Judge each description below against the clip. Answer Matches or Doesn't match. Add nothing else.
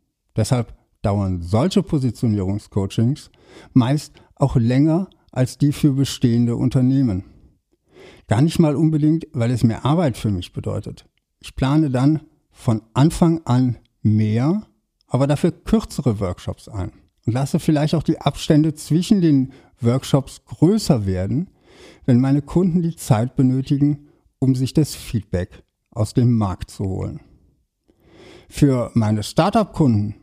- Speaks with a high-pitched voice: Doesn't match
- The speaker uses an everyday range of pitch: Doesn't match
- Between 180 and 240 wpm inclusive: Doesn't match